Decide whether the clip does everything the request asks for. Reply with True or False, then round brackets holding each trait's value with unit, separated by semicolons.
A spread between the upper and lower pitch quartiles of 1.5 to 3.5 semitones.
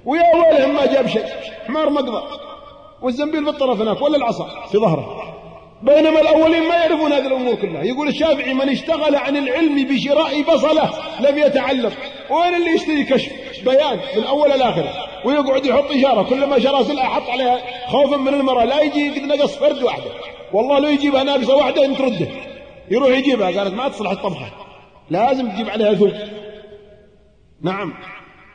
True (3.0 semitones)